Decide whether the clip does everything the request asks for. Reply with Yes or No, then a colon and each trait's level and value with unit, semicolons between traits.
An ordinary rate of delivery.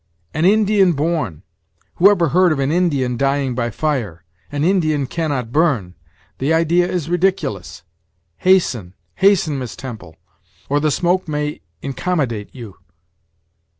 No: slow, 130 wpm